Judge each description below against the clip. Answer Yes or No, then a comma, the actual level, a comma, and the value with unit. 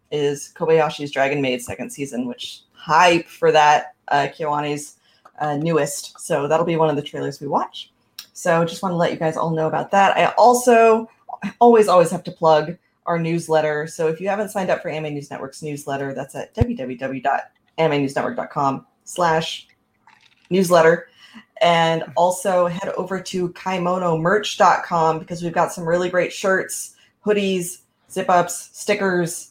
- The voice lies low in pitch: No, medium, 165 Hz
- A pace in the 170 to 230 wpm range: No, average, 155 wpm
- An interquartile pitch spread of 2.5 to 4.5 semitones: Yes, average, 3.5 semitones